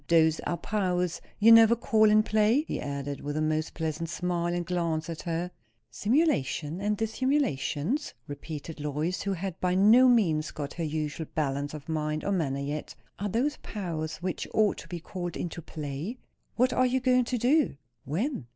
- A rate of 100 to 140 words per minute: No, average, 180 wpm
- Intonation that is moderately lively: No, wide, 5.7 semitones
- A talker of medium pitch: Yes, medium, 175 Hz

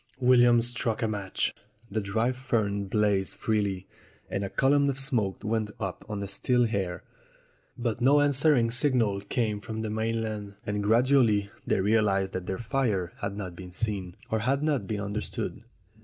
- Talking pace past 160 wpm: Yes, average, 170 wpm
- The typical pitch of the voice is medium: No, low, 110 Hz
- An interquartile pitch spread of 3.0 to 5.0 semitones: Yes, average, 3.4 semitones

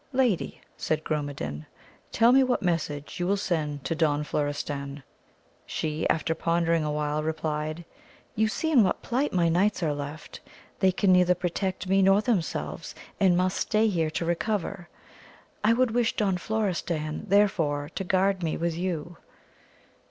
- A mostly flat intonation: No, average, 4.4 semitones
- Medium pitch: Yes, medium, 175 Hz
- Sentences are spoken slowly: No, average, 150 wpm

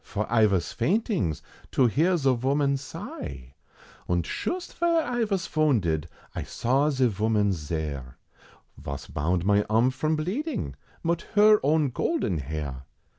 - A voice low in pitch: Yes, low, 125 Hz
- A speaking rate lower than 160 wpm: Yes, average, 140 wpm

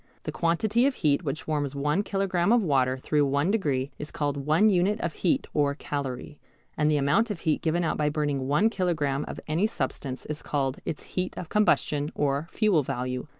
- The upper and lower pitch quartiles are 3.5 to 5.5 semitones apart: Yes, average, 4.4 semitones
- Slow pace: No, average, 195 wpm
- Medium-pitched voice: Yes, medium, 150 Hz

